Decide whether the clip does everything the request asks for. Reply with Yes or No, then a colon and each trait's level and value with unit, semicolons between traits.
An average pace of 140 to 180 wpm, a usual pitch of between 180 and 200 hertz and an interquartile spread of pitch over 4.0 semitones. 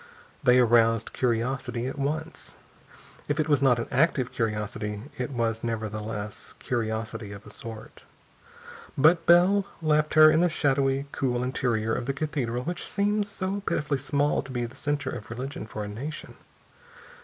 No: average, 155 wpm; low, 130 Hz; average, 4.9 semitones